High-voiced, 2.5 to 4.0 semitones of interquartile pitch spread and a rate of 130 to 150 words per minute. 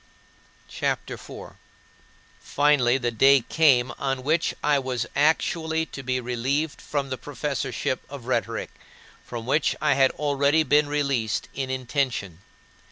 No: low, 135 Hz; average, 2.8 semitones; average, 140 wpm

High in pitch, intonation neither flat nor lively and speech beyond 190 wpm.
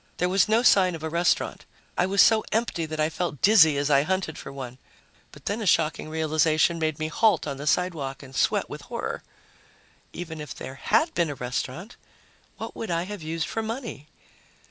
No: medium, 160 Hz; average, 4.1 semitones; average, 200 wpm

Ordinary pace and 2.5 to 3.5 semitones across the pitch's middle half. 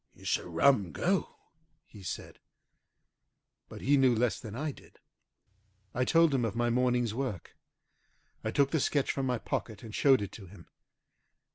No: average, 165 wpm; average, 4.1 semitones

